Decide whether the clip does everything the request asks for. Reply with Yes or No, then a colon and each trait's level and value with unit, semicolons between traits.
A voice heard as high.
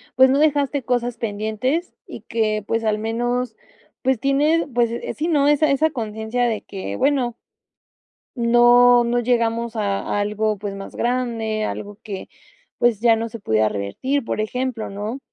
Yes: high, 235 Hz